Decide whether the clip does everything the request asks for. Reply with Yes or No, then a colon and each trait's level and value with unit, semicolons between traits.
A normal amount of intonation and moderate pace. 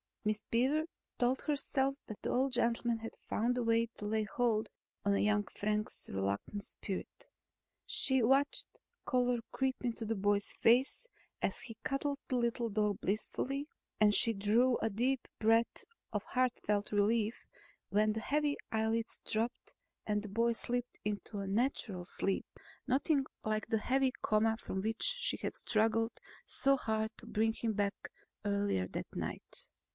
Yes: average, 3.0 semitones; average, 155 wpm